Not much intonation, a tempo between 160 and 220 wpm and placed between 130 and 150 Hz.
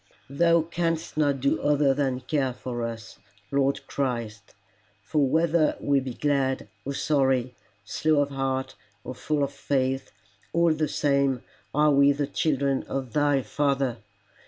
No: narrow, 2.0 semitones; average, 145 wpm; medium, 140 Hz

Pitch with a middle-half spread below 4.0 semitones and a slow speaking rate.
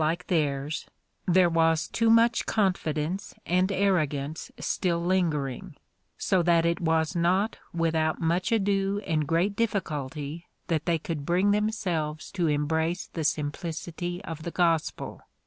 Yes: average, 3.0 semitones; slow, 130 wpm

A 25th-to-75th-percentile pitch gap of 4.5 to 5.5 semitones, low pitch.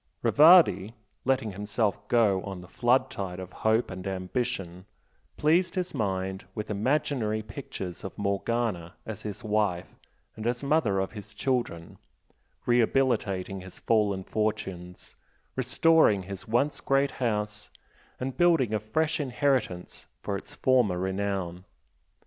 Yes: average, 5.0 semitones; low, 105 Hz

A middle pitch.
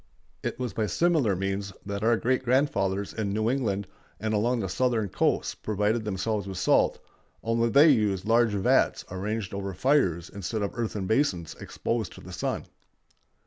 No: low, 105 Hz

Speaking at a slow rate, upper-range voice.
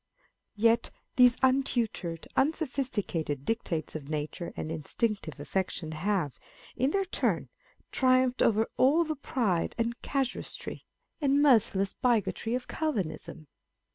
Yes: slow, 115 wpm; high, 230 Hz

